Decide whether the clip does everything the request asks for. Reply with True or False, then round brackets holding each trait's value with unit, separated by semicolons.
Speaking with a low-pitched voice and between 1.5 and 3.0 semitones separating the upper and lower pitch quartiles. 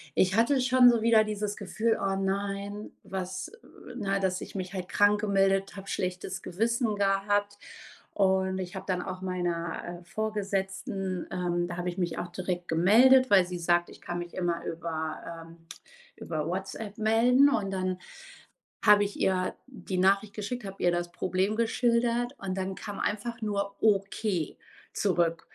False (195 Hz; 2.7 semitones)